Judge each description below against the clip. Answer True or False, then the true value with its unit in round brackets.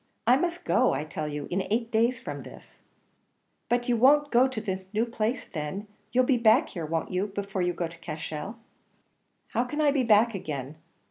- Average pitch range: False (5.9 semitones)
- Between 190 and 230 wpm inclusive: True (200 wpm)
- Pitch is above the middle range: True (215 Hz)